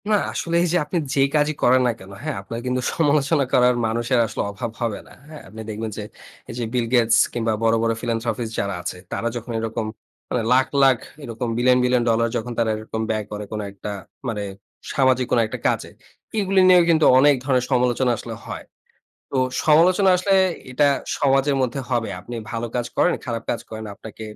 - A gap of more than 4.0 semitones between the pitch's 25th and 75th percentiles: No, average, 3.4 semitones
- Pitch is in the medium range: No, low, 120 Hz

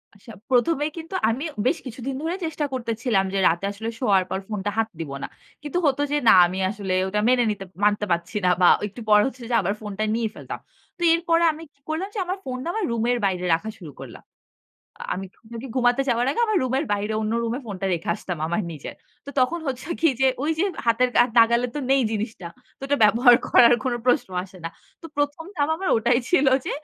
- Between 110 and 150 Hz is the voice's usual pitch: No, high, 240 Hz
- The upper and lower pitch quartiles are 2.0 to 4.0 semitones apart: No, wide, 5.5 semitones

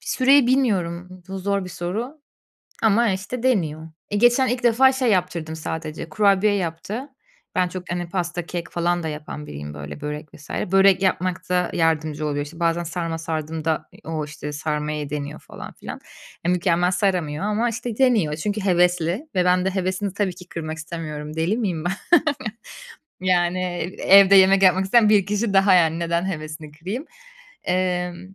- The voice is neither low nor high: Yes, medium, 180 Hz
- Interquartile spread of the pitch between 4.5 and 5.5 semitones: No, average, 3.7 semitones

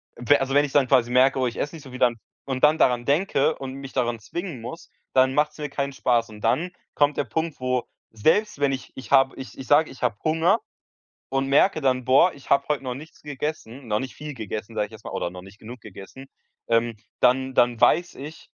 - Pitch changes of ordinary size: Yes, average, 3.4 semitones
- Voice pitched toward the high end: No, low, 135 Hz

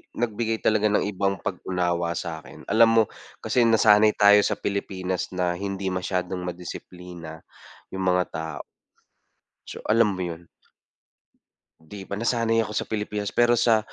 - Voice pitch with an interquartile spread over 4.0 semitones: No, average, 3.3 semitones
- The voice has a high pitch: No, low, 100 Hz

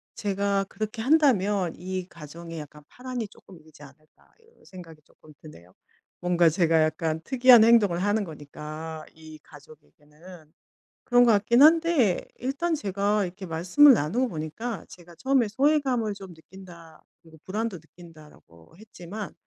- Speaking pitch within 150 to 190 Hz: Yes, medium, 185 Hz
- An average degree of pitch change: No, wide, 6.0 semitones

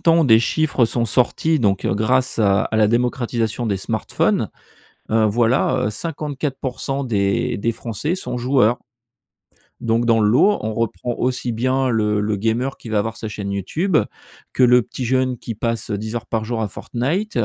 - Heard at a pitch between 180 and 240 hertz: No, low, 120 Hz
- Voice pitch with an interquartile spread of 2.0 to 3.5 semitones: Yes, average, 2.9 semitones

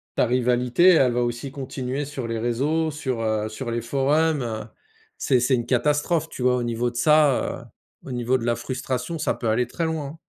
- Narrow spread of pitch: No, average, 3.5 semitones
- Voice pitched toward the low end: Yes, low, 125 Hz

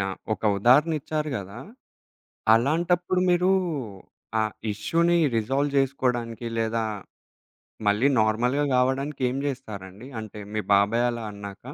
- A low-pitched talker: Yes, low, 120 Hz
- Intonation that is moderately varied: Yes, average, 4.8 semitones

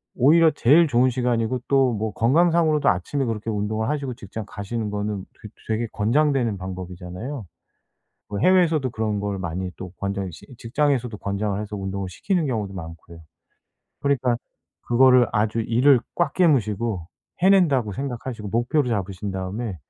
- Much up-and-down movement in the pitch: No, average, 5.0 semitones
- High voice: No, low, 115 Hz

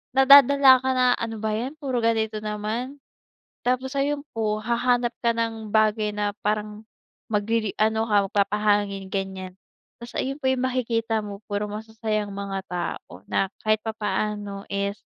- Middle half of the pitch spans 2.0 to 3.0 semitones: Yes, narrow, 2.6 semitones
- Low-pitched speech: No, high, 215 Hz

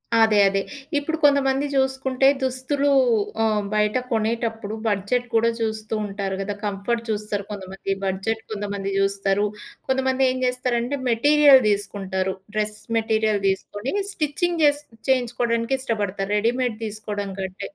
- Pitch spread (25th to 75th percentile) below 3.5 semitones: No, average, 4.2 semitones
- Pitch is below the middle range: No, high, 225 Hz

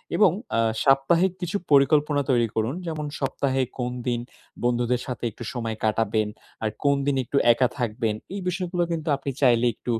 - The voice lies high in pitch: No, low, 135 Hz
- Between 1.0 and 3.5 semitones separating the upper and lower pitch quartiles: No, average, 4.2 semitones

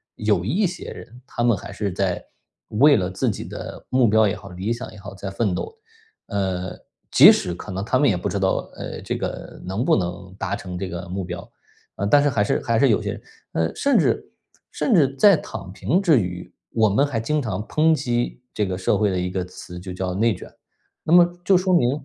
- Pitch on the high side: No, low, 105 Hz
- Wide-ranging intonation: Yes, wide, 5.7 semitones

